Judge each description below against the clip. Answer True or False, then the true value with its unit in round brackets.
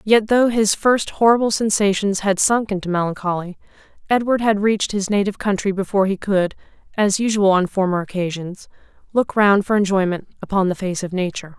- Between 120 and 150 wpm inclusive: False (170 wpm)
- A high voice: True (200 Hz)